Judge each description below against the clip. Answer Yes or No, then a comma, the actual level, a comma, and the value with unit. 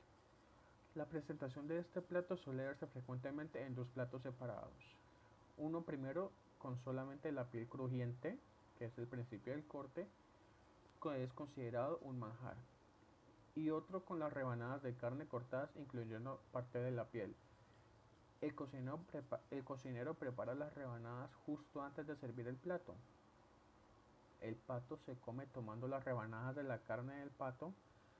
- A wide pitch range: No, average, 4.1 semitones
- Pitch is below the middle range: Yes, low, 130 Hz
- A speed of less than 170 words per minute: Yes, average, 145 wpm